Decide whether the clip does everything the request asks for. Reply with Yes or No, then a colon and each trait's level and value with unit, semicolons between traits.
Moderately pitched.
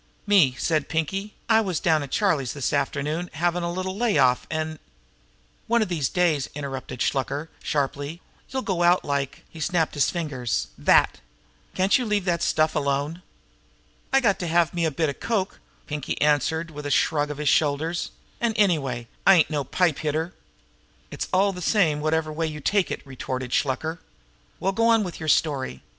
Yes: medium, 160 Hz